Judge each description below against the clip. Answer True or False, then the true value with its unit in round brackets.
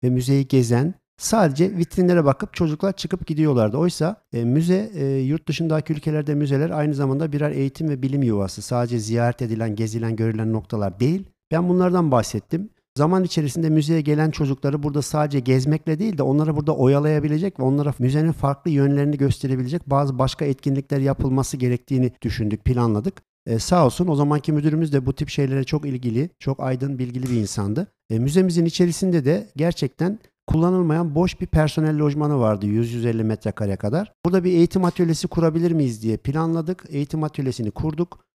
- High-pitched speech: False (145 Hz)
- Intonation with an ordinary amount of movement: True (4.3 semitones)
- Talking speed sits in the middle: False (160 wpm)